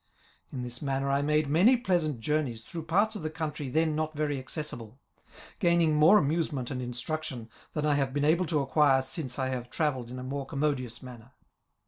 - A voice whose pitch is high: No, medium, 145 Hz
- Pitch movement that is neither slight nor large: Yes, average, 3.3 semitones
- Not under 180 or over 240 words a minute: Yes, average, 190 wpm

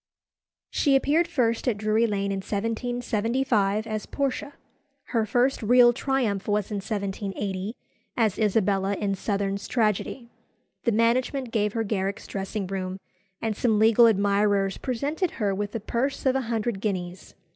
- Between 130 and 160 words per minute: Yes, average, 145 wpm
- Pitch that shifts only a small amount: No, average, 3.3 semitones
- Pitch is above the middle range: Yes, high, 215 Hz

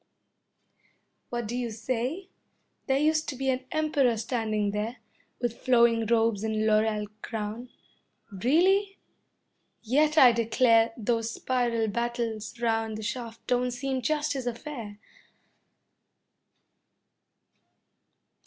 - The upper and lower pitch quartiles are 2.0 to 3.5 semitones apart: Yes, average, 2.7 semitones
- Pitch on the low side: No, high, 235 Hz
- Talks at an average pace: No, slow, 105 wpm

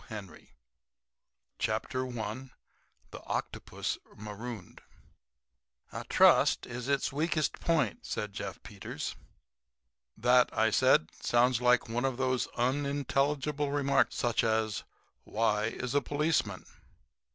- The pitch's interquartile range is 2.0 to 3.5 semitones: No, average, 3.9 semitones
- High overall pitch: No, low, 125 Hz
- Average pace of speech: No, slow, 110 wpm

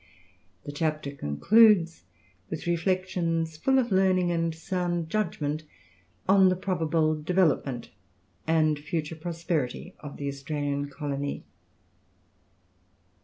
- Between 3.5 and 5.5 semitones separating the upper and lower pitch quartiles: Yes, average, 3.8 semitones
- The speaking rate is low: Yes, slow, 100 wpm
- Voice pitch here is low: No, medium, 165 Hz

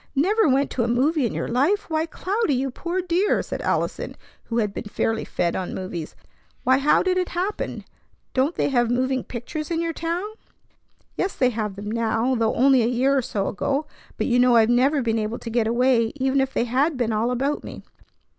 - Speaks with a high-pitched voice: Yes, very high, 255 Hz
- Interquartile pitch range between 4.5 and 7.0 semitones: Yes, average, 4.8 semitones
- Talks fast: Yes, fast, 210 wpm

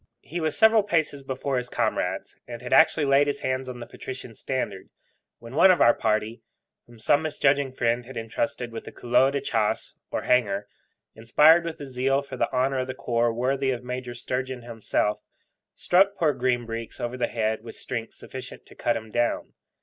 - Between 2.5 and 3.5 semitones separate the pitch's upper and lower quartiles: Yes, average, 2.9 semitones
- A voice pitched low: Yes, low, 125 Hz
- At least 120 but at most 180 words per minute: No, average, 195 wpm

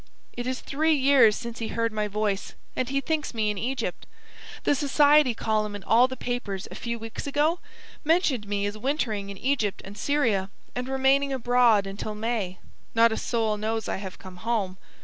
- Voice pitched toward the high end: Yes, high, 230 Hz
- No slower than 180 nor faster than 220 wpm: Yes, average, 190 wpm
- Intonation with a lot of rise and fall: No, average, 4.3 semitones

